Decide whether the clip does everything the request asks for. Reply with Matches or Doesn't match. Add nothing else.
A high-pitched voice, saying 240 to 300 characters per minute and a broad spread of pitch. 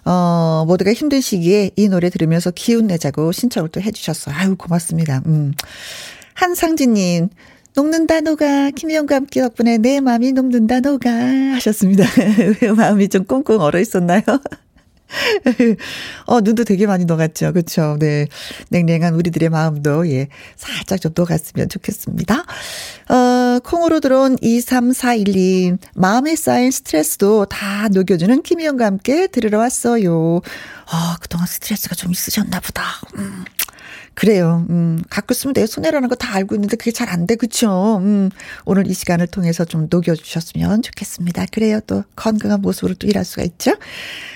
Doesn't match